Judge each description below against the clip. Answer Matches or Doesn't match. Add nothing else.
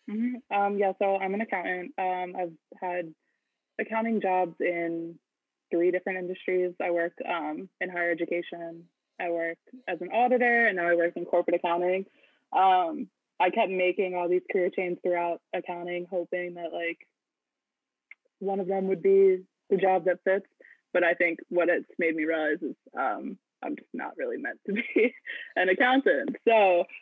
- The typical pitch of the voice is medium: Matches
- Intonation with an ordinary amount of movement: Doesn't match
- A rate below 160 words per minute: Doesn't match